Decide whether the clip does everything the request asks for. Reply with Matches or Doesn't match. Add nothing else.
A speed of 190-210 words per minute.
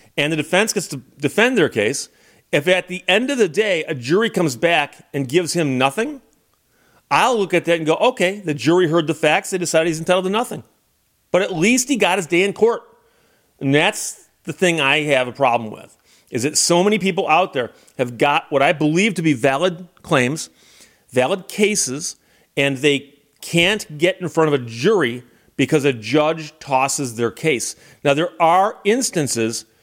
Matches